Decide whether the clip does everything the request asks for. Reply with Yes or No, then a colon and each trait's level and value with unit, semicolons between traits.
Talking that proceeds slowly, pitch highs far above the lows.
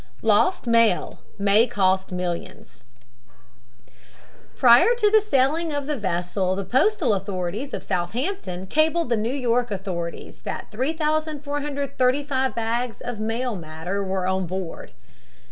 Yes: slow, 120 wpm; wide, 7.2 semitones